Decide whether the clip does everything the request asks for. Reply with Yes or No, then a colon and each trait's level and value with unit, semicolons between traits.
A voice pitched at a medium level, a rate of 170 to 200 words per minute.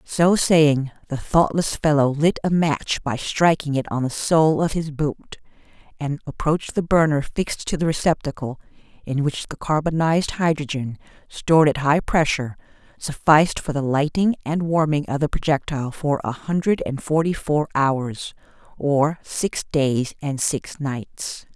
No: medium, 150 Hz; average, 155 wpm